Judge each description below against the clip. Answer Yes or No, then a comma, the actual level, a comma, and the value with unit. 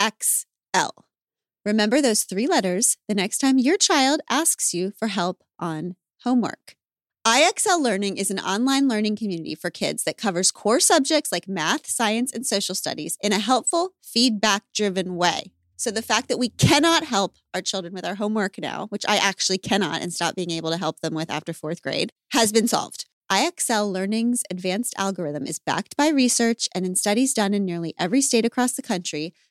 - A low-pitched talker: No, high, 205 Hz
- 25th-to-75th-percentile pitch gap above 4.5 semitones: Yes, average, 5.3 semitones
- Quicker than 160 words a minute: Yes, average, 185 wpm